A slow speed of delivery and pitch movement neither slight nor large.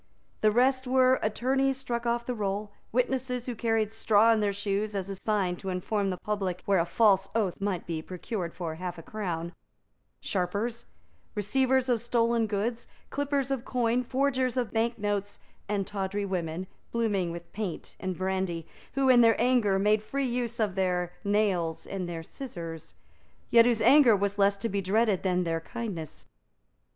No: average, 170 wpm; average, 4.0 semitones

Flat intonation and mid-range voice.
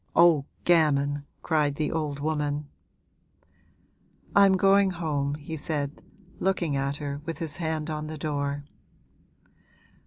Yes: narrow, 2.2 semitones; medium, 150 Hz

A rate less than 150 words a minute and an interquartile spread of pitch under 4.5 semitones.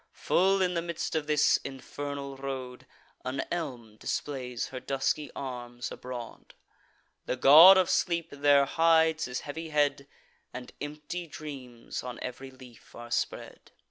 Yes: average, 140 wpm; average, 3.8 semitones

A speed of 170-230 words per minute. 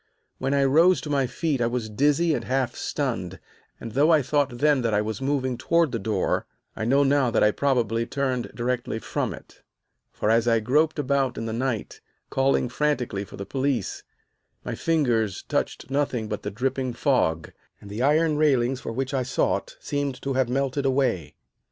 Yes: average, 190 wpm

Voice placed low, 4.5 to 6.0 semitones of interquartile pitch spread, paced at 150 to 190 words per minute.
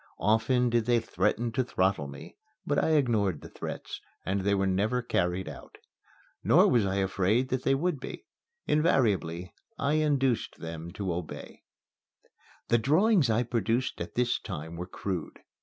Yes: low, 110 Hz; wide, 5.4 semitones; average, 155 wpm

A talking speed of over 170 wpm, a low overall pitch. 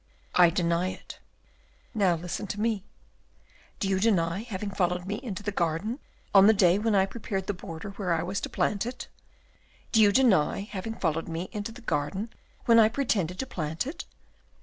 No: average, 185 wpm; high, 195 Hz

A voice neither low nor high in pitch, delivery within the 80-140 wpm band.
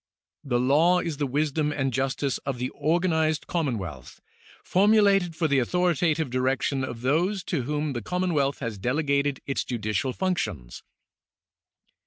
Yes: medium, 145 Hz; slow, 135 wpm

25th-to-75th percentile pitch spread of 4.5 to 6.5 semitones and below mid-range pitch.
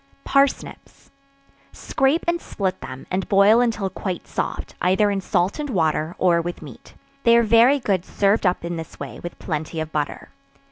No: average, 5.2 semitones; high, 190 Hz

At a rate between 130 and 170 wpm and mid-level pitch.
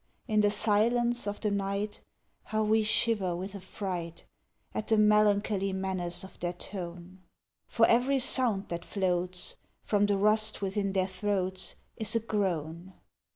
No: average, 145 wpm; high, 200 Hz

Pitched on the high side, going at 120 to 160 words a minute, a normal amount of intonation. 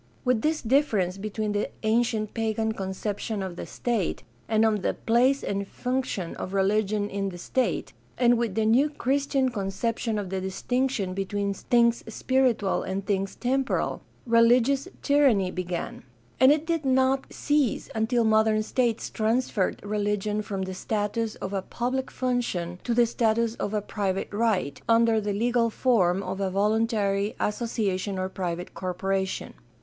Yes: high, 215 Hz; average, 150 wpm; average, 3.6 semitones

